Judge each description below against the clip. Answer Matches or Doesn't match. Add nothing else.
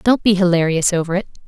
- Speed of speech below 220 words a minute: Matches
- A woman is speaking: Matches